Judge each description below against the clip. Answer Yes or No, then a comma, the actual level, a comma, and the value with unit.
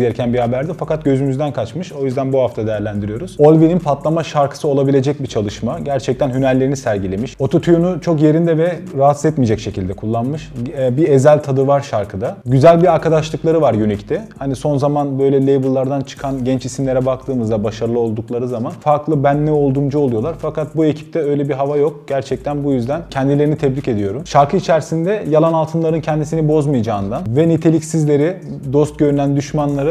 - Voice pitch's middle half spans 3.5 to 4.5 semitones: No, average, 2.9 semitones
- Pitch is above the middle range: No, medium, 140 Hz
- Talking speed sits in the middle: No, fast, 160 wpm